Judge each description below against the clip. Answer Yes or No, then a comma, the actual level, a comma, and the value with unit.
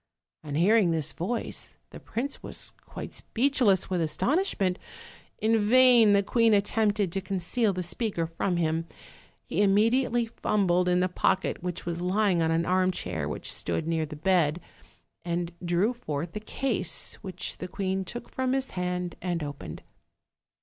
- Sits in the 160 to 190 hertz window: Yes, medium, 185 Hz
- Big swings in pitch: No, average, 4.2 semitones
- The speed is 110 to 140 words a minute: No, average, 155 wpm